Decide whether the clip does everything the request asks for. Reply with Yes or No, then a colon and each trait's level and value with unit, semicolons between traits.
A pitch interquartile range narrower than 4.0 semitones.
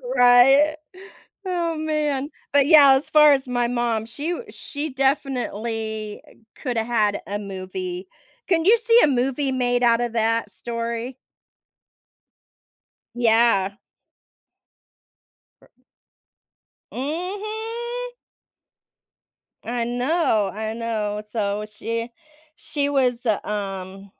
No: average, 4.9 semitones